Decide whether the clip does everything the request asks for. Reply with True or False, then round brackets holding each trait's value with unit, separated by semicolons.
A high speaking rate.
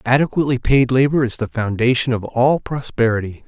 False (155 wpm)